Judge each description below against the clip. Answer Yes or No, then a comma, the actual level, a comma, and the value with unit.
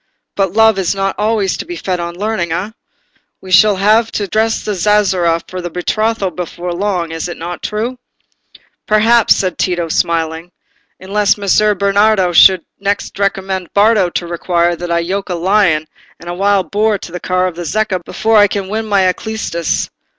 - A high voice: Yes, high, 195 Hz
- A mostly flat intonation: No, average, 3.2 semitones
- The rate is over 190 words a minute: No, average, 180 wpm